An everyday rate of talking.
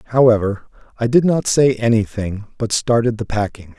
Yes: average, 160 wpm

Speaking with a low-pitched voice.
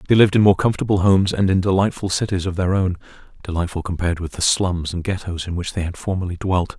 Yes: very low, 90 Hz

